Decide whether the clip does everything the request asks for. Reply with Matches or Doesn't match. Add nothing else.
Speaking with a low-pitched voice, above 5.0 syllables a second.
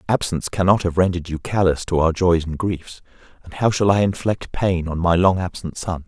Matches